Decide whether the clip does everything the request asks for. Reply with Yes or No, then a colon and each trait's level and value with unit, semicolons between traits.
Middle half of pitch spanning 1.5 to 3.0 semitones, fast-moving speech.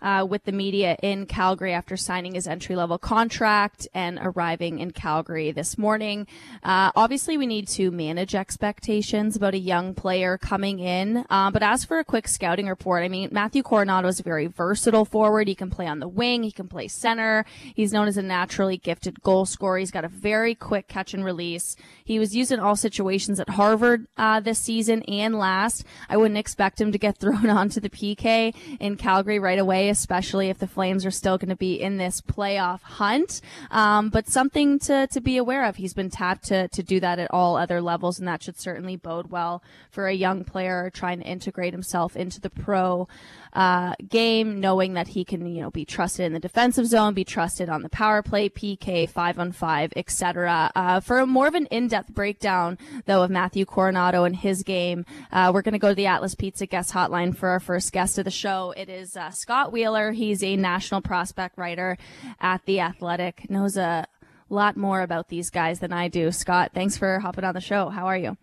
Yes: average, 2.7 semitones; fast, 210 wpm